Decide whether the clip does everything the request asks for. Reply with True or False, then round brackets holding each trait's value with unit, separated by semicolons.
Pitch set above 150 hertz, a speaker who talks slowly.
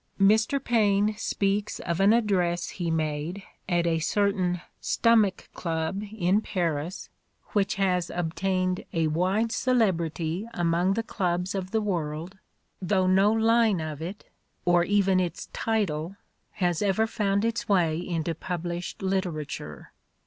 False (185 Hz; 150 wpm)